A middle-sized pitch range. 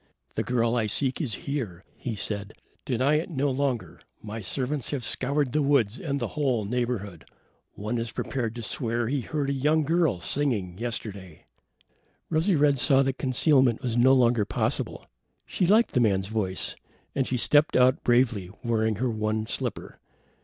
Yes: average, 4.2 semitones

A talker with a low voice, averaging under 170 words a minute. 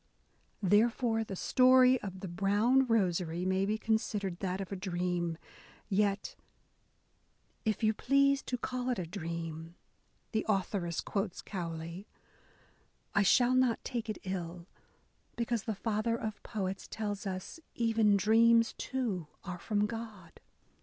No: high, 205 Hz; slow, 135 wpm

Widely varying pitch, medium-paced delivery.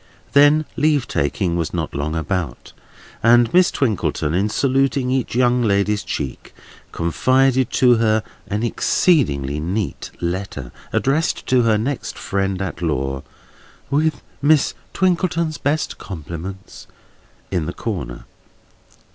No: wide, 8.0 semitones; slow, 120 wpm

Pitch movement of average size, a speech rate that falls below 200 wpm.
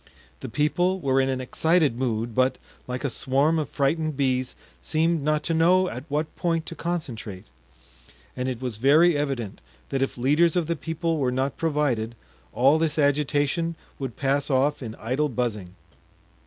Yes: average, 3.9 semitones; average, 170 wpm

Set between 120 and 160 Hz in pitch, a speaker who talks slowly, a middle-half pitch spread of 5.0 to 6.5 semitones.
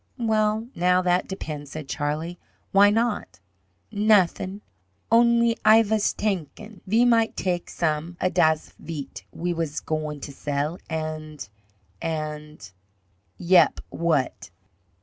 No: medium, 170 Hz; slow, 120 wpm; wide, 5.5 semitones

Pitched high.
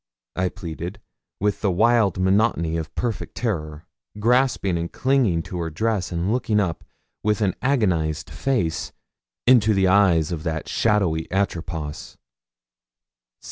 No: very low, 95 Hz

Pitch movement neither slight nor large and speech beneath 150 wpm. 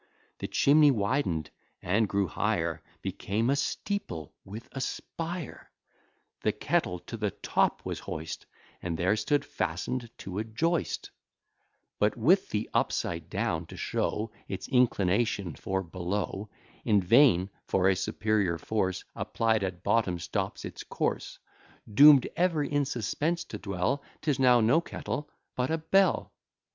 No: wide, 6.8 semitones; average, 140 wpm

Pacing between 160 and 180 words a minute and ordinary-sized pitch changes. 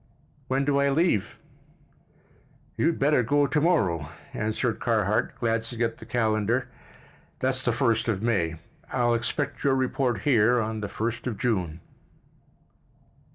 No: slow, 135 wpm; average, 3.6 semitones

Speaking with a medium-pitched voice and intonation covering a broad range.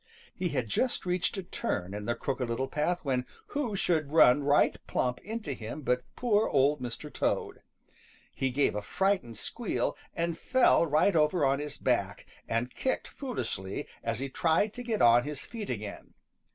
Yes: medium, 145 Hz; wide, 6.9 semitones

